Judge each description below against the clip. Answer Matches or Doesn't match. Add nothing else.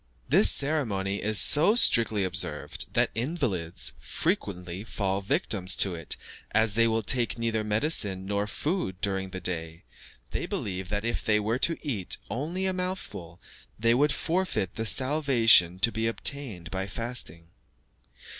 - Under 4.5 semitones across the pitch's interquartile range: Doesn't match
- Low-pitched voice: Matches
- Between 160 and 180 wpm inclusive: Doesn't match